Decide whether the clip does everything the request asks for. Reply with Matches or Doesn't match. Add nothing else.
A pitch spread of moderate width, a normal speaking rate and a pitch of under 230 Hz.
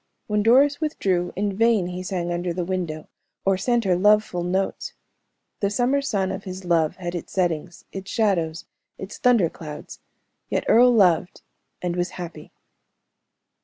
Matches